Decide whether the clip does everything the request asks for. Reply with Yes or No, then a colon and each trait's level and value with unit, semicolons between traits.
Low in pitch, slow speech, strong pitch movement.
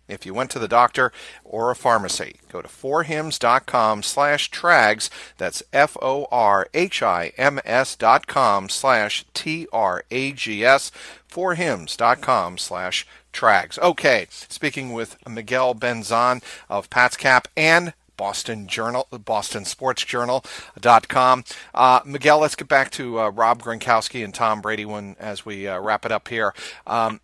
No: low, 120 Hz; slow, 125 wpm; average, 3.4 semitones